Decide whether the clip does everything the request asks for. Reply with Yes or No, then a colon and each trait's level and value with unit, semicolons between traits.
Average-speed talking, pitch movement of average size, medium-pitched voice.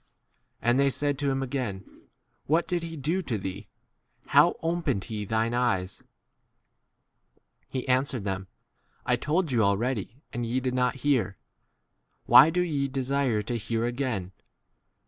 No: average, 145 wpm; average, 4.2 semitones; low, 125 Hz